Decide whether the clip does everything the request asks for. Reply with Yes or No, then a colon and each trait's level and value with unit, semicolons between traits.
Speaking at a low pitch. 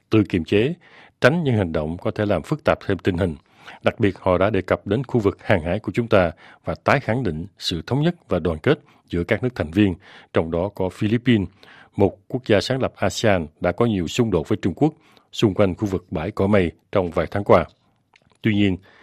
Yes: low, 105 Hz